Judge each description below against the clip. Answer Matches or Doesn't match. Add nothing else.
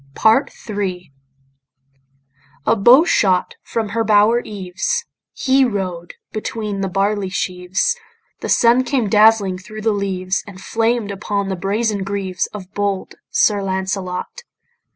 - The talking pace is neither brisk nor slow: Doesn't match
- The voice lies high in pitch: Matches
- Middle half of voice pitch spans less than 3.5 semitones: Matches